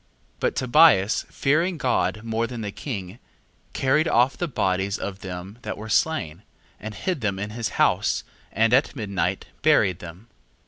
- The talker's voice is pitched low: Yes, low, 110 Hz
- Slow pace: No, average, 165 wpm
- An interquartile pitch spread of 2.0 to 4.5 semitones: No, average, 5.3 semitones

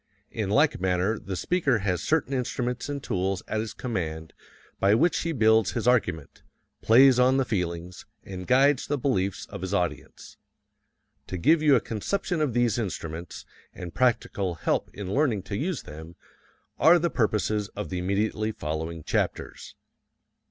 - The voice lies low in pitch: Yes, low, 110 Hz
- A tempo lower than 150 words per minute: No, average, 160 wpm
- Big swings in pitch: Yes, wide, 6.1 semitones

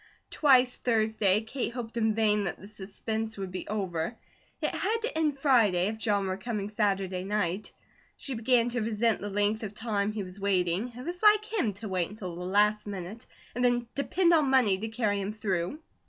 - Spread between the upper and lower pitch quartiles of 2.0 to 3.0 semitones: No, average, 3.6 semitones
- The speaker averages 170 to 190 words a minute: No, average, 200 wpm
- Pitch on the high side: Yes, high, 215 Hz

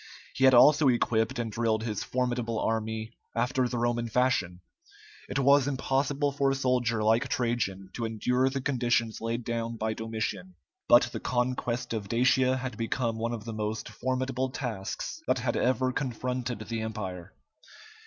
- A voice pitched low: Yes, low, 120 Hz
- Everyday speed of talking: Yes, average, 160 wpm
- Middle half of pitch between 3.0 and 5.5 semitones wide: No, narrow, 2.5 semitones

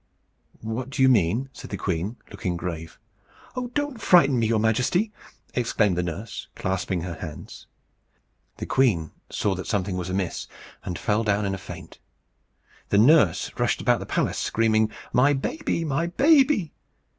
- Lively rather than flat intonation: Yes, wide, 6.8 semitones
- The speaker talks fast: No, average, 155 wpm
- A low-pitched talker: Yes, low, 110 Hz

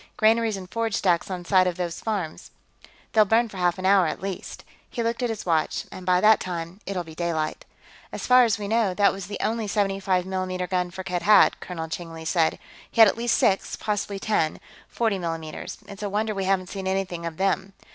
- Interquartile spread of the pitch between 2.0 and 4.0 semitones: Yes, average, 3.0 semitones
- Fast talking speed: Yes, fast, 215 wpm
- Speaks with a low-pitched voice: No, high, 190 Hz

